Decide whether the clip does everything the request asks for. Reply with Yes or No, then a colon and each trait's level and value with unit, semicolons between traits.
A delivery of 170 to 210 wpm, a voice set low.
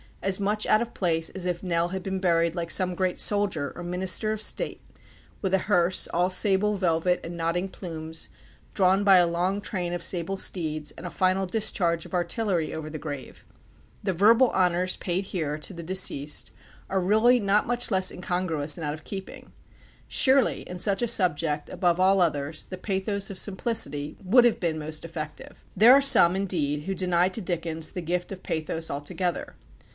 No: average, 185 wpm; medium, 180 Hz